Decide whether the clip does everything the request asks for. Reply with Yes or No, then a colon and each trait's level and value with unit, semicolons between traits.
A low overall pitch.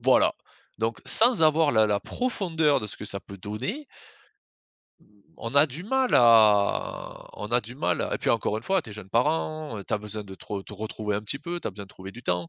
Yes: low, 115 Hz